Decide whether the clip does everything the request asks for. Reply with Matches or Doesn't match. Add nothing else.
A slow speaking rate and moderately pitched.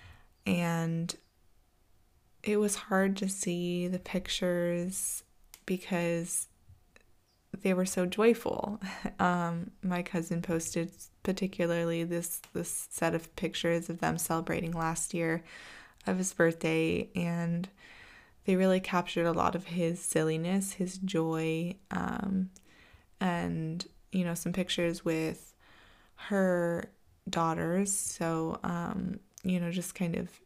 Matches